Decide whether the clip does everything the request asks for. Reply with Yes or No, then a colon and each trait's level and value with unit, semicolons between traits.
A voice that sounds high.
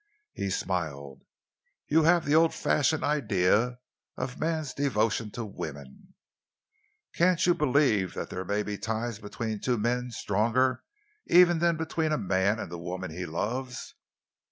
No: low, 115 Hz